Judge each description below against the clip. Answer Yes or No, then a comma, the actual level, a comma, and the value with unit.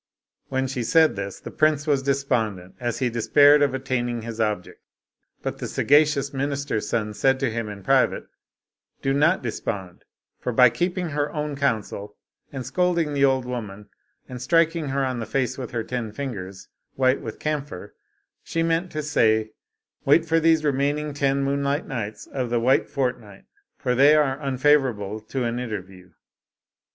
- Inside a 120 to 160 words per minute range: No, average, 175 wpm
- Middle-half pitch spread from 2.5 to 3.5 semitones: No, average, 4.2 semitones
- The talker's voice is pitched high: No, low, 135 Hz